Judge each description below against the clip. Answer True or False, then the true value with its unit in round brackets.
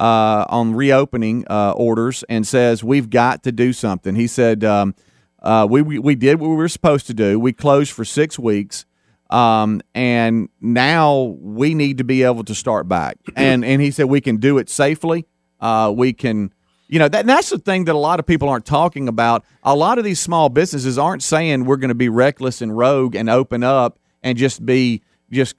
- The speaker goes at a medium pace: False (210 wpm)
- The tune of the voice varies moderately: True (3.9 semitones)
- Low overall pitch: True (125 Hz)